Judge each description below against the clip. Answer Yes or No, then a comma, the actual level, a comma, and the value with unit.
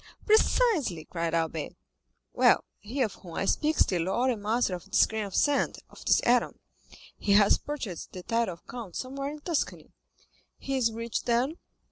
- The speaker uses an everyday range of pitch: No, wide, 6.5 semitones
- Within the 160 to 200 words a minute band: Yes, average, 180 wpm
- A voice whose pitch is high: Yes, high, 230 Hz